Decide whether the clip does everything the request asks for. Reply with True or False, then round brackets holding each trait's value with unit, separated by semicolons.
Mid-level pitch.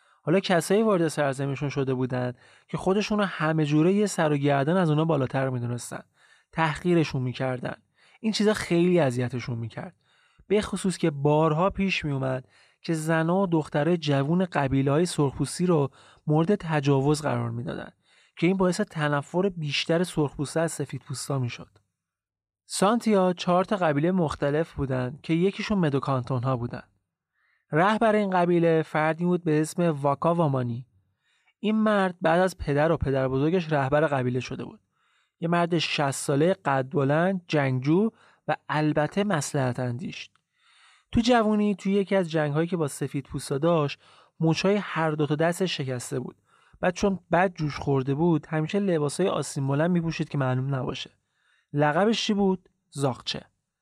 True (155 Hz)